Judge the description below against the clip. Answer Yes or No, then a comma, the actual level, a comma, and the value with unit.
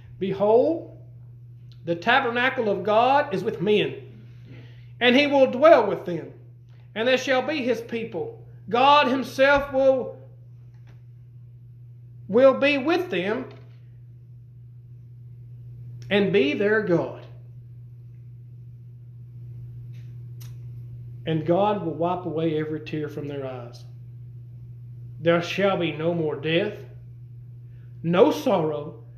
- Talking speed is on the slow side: Yes, slow, 100 wpm